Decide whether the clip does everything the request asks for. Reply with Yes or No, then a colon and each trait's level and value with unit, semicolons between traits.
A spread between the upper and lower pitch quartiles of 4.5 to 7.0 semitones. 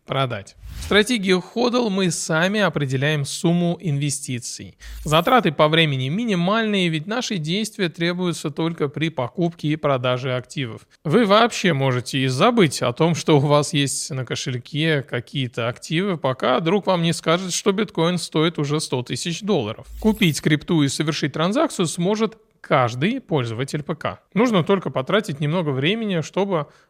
Yes: average, 4.9 semitones